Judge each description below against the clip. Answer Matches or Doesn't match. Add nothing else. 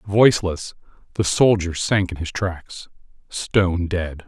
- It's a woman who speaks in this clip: Doesn't match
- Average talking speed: Doesn't match